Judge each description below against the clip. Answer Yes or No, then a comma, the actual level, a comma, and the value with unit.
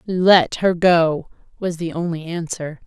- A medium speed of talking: Yes, average, 145 wpm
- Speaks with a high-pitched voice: No, medium, 170 Hz